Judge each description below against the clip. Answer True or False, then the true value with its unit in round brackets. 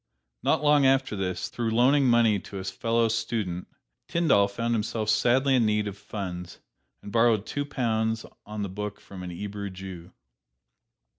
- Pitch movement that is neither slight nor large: True (3.0 semitones)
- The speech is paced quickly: False (160 wpm)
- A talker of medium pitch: False (110 Hz)